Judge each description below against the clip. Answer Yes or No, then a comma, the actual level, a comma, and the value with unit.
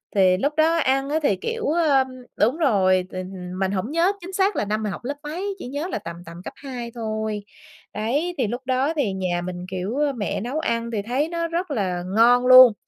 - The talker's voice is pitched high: Yes, high, 245 Hz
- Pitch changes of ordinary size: No, wide, 6.9 semitones